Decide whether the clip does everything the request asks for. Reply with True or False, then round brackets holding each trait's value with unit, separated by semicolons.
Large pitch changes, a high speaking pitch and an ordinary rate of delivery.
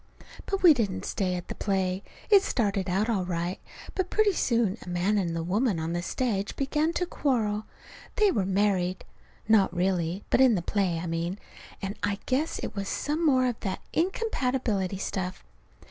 True (5.9 semitones; 200 Hz; 180 wpm)